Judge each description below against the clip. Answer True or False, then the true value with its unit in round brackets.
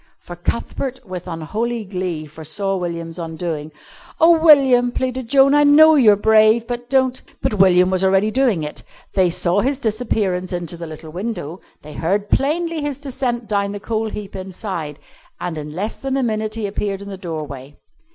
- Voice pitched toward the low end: False (205 Hz)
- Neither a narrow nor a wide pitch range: False (5.9 semitones)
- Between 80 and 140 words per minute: False (180 wpm)